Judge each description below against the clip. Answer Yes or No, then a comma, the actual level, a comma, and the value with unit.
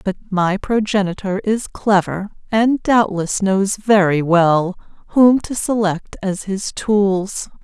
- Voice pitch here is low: No, high, 200 Hz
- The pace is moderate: No, slow, 125 wpm